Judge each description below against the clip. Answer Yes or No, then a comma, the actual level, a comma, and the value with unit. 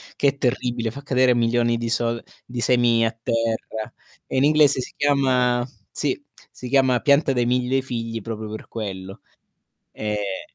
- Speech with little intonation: Yes, narrow, 2.2 semitones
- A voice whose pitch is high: No, low, 120 Hz